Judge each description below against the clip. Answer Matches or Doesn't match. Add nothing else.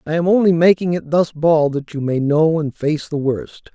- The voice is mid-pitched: Matches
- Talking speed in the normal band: Doesn't match